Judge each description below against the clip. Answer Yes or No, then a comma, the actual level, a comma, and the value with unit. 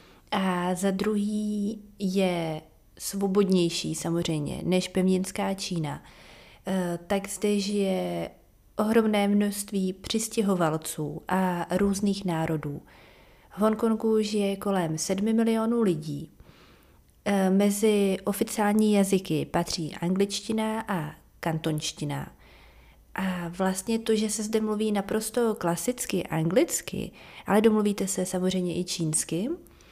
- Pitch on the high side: Yes, high, 195 Hz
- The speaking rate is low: Yes, slow, 100 wpm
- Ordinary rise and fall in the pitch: Yes, average, 3.4 semitones